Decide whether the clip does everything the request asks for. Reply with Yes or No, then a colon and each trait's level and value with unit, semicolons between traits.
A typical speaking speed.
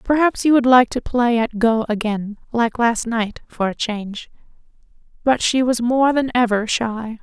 Yes: average, 185 wpm